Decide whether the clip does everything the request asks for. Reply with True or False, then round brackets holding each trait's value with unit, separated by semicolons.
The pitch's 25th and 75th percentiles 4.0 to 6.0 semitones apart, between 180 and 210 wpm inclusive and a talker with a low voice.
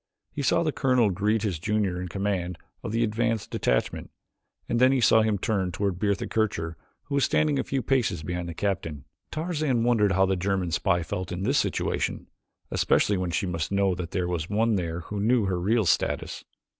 True (4.4 semitones; 200 wpm; 100 Hz)